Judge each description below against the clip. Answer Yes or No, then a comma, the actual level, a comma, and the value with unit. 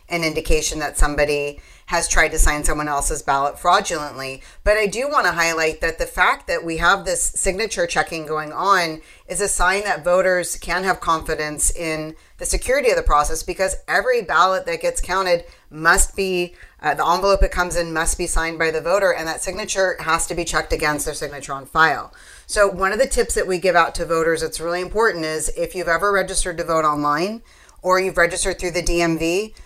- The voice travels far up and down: No, average, 3.1 semitones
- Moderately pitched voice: Yes, medium, 170 Hz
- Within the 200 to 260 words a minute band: Yes, fast, 205 wpm